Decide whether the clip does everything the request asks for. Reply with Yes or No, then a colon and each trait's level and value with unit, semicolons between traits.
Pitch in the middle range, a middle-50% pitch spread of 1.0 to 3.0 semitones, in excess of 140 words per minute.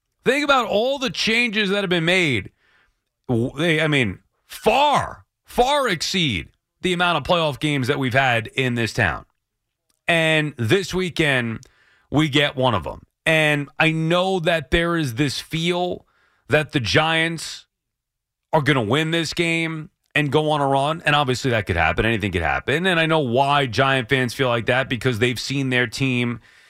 No: medium, 150 Hz; average, 4.7 semitones; average, 175 wpm